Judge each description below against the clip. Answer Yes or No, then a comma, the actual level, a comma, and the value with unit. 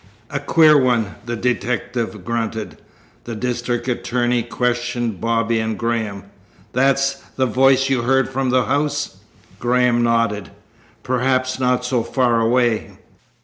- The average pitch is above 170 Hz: No, low, 120 Hz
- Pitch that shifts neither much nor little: No, narrow, 1.8 semitones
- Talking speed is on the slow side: Yes, slow, 125 wpm